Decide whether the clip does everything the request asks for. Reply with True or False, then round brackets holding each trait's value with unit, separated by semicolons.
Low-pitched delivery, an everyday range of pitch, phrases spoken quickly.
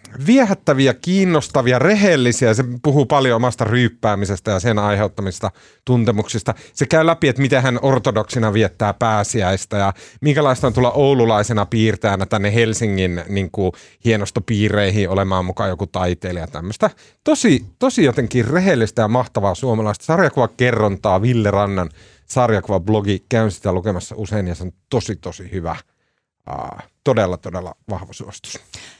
False (110 Hz; 4.2 semitones; 135 wpm)